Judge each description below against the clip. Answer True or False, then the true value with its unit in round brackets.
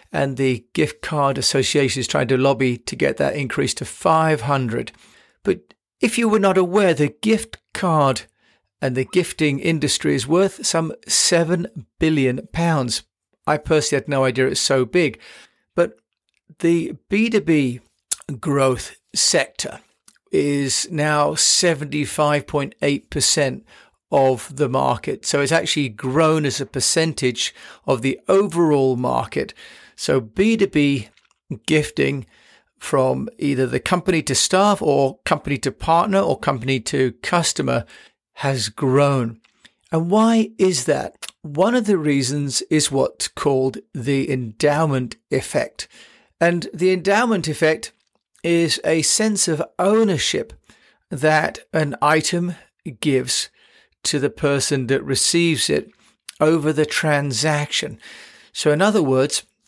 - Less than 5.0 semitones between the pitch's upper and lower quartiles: True (4.1 semitones)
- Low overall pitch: False (150 Hz)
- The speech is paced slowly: True (125 wpm)